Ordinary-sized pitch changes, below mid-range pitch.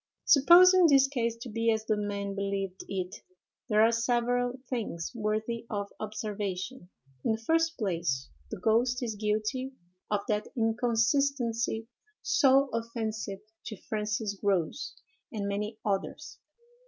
No: average, 3.2 semitones; high, 220 Hz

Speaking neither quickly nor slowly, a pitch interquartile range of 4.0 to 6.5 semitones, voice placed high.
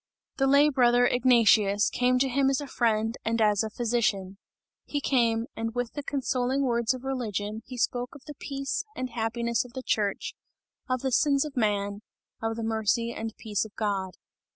No: average, 185 wpm; average, 2.9 semitones; high, 235 Hz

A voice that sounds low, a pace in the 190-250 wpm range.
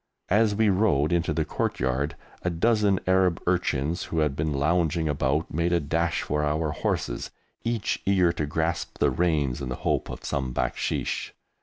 No: very low, 80 Hz; average, 170 wpm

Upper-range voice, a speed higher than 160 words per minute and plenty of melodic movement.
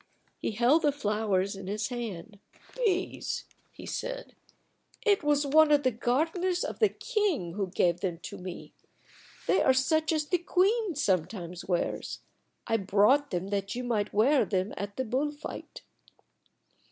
No: high, 245 Hz; average, 155 wpm; wide, 7.9 semitones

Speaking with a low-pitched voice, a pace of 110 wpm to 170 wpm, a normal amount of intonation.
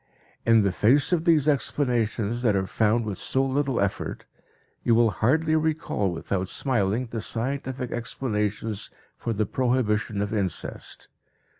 Yes: low, 115 Hz; average, 140 wpm; average, 4.1 semitones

